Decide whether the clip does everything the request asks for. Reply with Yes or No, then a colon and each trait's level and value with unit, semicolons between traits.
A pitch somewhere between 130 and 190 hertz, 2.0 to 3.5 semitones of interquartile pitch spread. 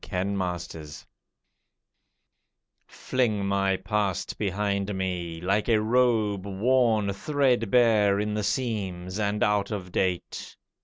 No: low, 100 Hz; narrow, 2.4 semitones